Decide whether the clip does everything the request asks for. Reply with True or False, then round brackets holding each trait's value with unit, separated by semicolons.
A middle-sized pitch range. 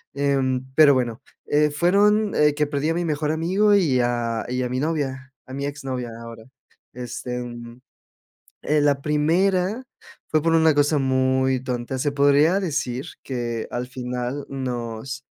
True (3.5 semitones)